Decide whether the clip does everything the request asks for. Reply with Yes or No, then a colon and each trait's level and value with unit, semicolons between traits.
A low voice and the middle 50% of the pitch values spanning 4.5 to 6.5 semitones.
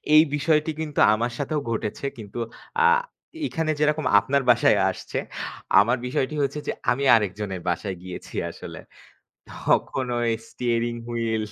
Yes: low, 120 Hz; average, 5.2 semitones